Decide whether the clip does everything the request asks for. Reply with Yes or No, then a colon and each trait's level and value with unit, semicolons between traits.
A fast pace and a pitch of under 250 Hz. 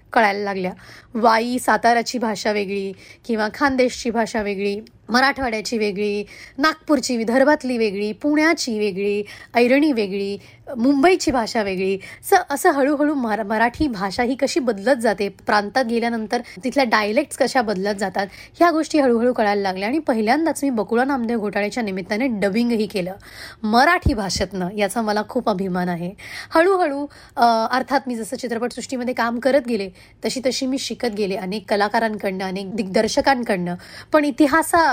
Yes: fast, 135 wpm; high, 235 Hz